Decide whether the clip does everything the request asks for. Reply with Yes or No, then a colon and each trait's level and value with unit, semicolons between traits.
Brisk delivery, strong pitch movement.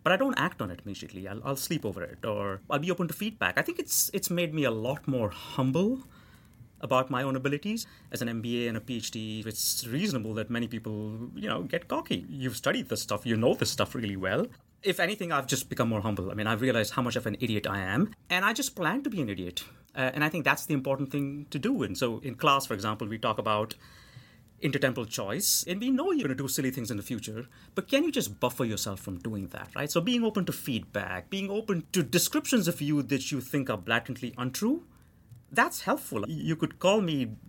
Yes: fast, 240 wpm; wide, 6.7 semitones